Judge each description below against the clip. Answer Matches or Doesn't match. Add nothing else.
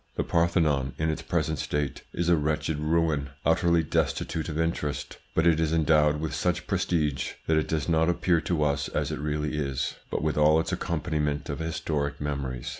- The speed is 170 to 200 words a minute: Matches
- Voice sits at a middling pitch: Doesn't match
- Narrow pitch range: Matches